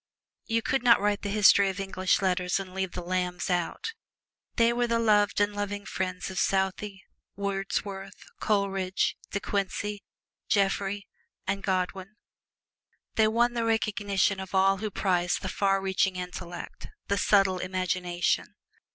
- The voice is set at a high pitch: Yes, high, 195 Hz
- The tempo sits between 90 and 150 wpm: Yes, average, 145 wpm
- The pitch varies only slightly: Yes, narrow, 1.8 semitones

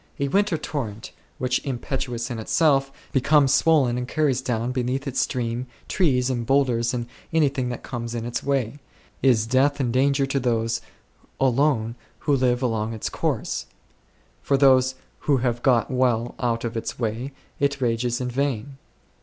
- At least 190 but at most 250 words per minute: No, average, 160 wpm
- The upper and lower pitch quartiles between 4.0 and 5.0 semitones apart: No, narrow, 2.6 semitones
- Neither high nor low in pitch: No, low, 125 Hz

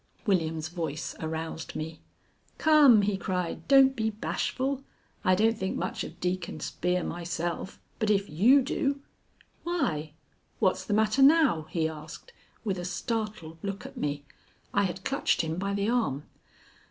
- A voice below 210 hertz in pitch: Yes, high, 190 Hz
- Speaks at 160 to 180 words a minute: No, average, 150 wpm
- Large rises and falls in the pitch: Yes, wide, 5.7 semitones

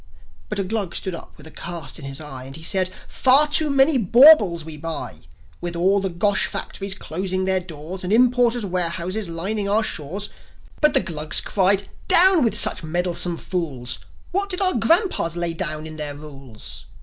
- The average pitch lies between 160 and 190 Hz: Yes, medium, 185 Hz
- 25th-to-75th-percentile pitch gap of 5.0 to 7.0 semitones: Yes, average, 5.3 semitones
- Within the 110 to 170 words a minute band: No, average, 185 wpm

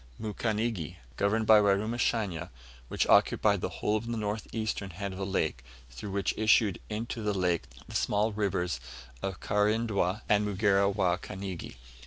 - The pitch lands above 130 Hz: No, low, 105 Hz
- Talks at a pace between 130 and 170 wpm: Yes, average, 155 wpm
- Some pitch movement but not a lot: No, narrow, 2.3 semitones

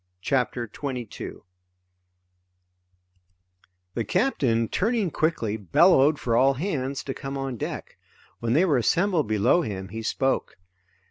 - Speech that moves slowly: Yes, slow, 120 wpm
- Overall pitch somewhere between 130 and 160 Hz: Yes, low, 135 Hz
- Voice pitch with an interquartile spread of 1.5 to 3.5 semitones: No, wide, 5.6 semitones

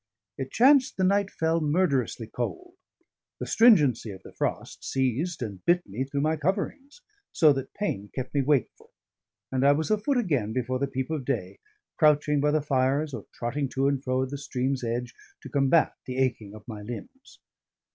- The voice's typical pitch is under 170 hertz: Yes, medium, 140 Hz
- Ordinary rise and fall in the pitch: Yes, average, 4.2 semitones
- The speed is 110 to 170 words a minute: No, average, 185 wpm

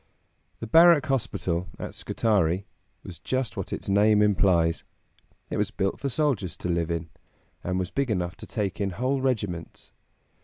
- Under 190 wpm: Yes, average, 160 wpm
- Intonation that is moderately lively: No, wide, 5.7 semitones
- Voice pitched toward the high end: No, low, 100 Hz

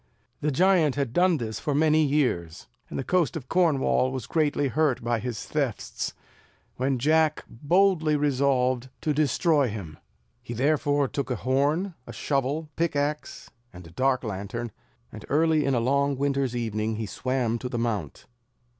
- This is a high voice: No, medium, 140 Hz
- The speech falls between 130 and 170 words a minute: Yes, average, 160 wpm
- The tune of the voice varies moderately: Yes, average, 4.1 semitones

